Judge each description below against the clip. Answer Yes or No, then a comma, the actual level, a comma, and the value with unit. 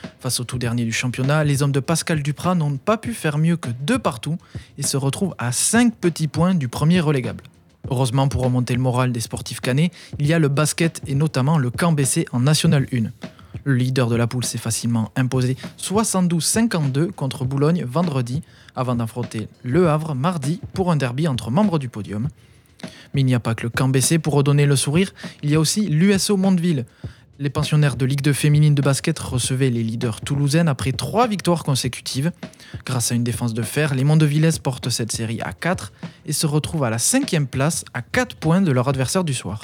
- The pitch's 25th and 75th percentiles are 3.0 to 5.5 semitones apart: Yes, average, 4.6 semitones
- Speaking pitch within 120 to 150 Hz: Yes, medium, 140 Hz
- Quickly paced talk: No, average, 205 wpm